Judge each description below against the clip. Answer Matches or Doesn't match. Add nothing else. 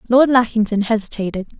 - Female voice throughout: Matches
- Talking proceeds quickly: Doesn't match